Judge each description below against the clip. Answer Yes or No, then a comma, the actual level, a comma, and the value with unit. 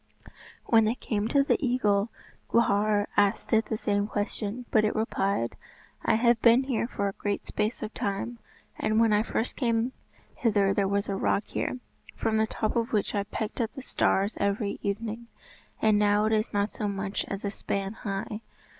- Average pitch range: No, narrow, 2.1 semitones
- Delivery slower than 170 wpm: No, average, 190 wpm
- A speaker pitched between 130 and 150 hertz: No, high, 215 Hz